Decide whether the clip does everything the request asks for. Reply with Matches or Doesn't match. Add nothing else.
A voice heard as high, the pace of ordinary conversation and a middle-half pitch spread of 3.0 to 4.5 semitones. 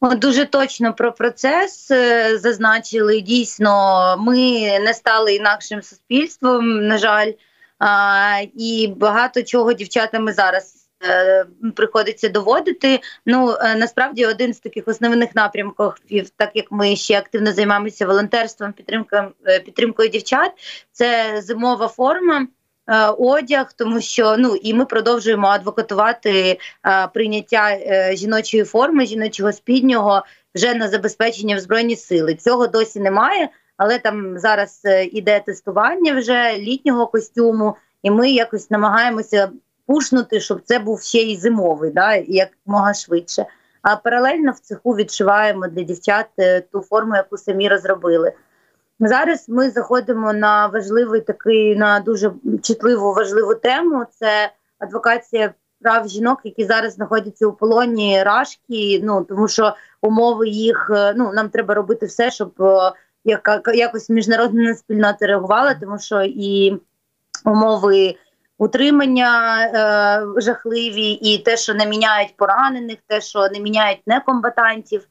Doesn't match